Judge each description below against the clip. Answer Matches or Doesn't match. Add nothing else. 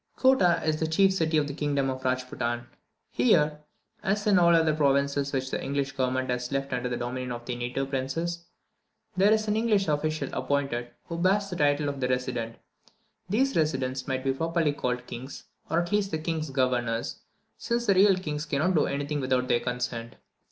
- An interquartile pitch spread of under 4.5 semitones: Doesn't match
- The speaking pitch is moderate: Matches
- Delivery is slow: Doesn't match